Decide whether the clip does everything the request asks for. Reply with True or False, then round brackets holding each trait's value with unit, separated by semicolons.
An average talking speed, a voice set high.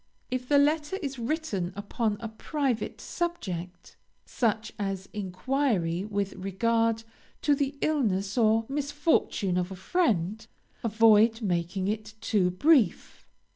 False (115 wpm; 220 Hz)